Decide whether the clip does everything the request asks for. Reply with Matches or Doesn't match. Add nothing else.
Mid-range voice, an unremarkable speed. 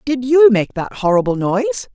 Doesn't match